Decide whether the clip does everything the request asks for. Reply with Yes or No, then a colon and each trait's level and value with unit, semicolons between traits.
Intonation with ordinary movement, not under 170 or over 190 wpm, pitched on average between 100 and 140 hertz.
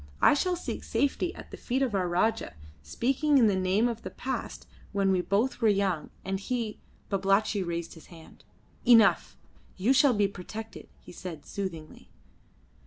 No: average, 4.7 semitones; average, 175 wpm; high, 205 Hz